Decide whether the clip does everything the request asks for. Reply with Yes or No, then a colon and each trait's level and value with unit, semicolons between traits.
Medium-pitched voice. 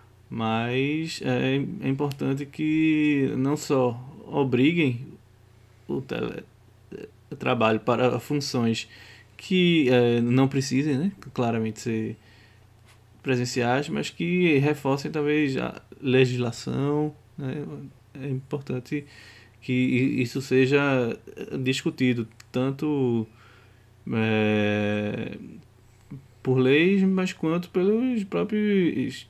No: low, 130 Hz